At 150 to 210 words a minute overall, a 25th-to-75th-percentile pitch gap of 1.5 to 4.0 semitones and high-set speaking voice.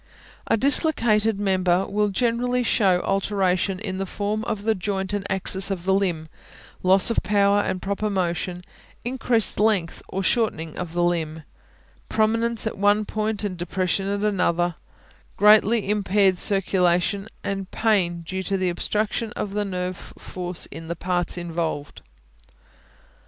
No: average, 140 wpm; average, 2.8 semitones; high, 195 Hz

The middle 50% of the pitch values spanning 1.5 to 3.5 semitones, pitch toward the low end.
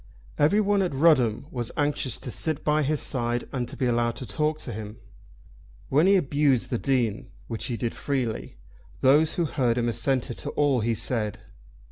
No: average, 4.1 semitones; low, 130 Hz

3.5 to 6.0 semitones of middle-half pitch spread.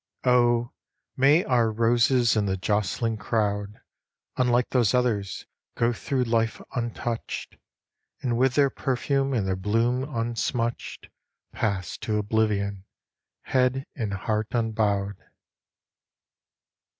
No: average, 3.0 semitones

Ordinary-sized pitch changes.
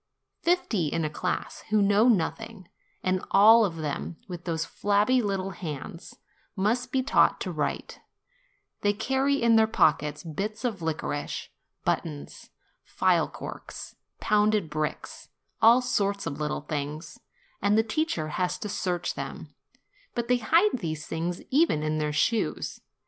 No: wide, 5.9 semitones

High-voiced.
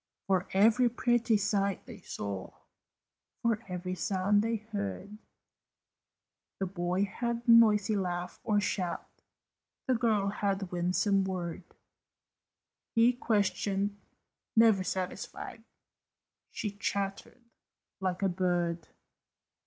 Yes: high, 200 Hz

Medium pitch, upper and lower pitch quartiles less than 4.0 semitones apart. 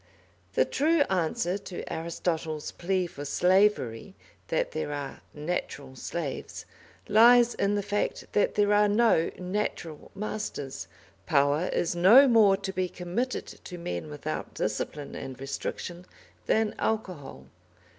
No: medium, 180 Hz; wide, 5.5 semitones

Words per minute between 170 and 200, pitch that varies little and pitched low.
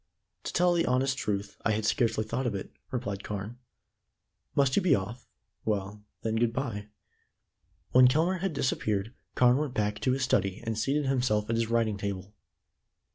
No: average, 175 wpm; average, 4.0 semitones; low, 115 Hz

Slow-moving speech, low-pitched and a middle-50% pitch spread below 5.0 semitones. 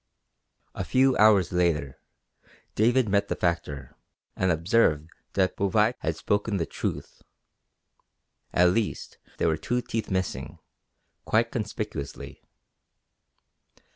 Yes: slow, 105 wpm; low, 100 Hz; average, 4.5 semitones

